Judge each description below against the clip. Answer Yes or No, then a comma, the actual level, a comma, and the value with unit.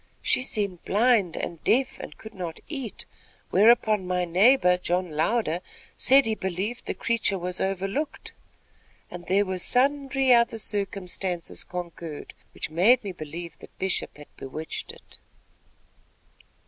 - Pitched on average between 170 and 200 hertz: Yes, high, 190 Hz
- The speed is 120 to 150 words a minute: Yes, slow, 135 wpm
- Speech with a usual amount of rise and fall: Yes, average, 4.9 semitones